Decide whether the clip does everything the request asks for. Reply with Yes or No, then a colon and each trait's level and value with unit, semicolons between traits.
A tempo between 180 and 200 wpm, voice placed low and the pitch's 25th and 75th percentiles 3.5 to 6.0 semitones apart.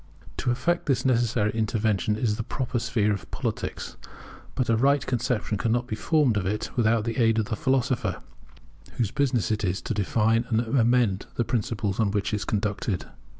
No: average, 185 wpm; low, 115 Hz; narrow, 2.6 semitones